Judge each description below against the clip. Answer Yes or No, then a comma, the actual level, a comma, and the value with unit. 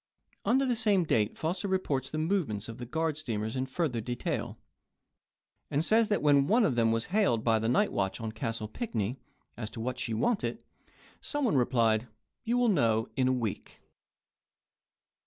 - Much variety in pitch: Yes, wide, 8.7 semitones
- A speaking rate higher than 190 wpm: No, average, 180 wpm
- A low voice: Yes, low, 130 Hz